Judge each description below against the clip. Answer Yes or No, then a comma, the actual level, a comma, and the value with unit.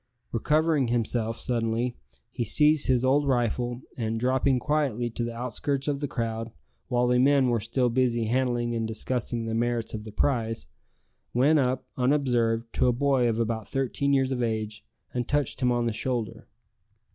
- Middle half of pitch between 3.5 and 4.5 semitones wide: No, narrow, 2.4 semitones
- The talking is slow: No, average, 170 wpm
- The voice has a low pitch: Yes, low, 120 Hz